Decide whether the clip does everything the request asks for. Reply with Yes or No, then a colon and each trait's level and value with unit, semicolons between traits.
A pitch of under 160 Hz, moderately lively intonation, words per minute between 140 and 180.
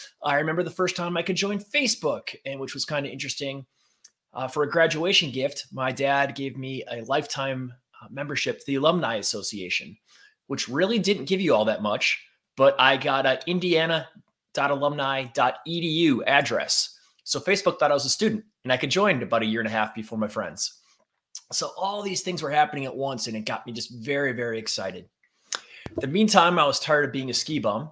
No: medium, 140 Hz; average, 4.6 semitones; average, 200 wpm